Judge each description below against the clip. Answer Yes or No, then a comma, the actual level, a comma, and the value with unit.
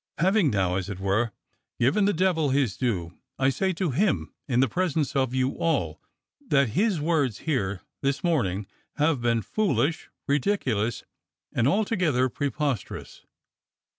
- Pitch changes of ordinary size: No, wide, 6.1 semitones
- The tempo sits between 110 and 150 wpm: Yes, average, 140 wpm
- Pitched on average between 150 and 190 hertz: No, low, 135 Hz